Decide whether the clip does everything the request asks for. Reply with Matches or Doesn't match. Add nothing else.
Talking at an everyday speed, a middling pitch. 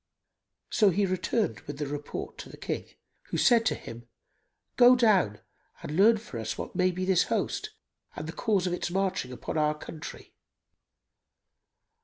Matches